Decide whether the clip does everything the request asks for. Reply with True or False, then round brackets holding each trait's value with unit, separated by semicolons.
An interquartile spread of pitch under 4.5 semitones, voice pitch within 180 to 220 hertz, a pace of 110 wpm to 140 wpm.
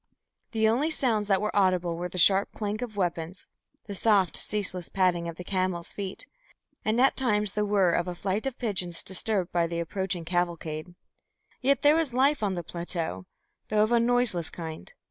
False (3.9 semitones; 190 Hz; 185 wpm)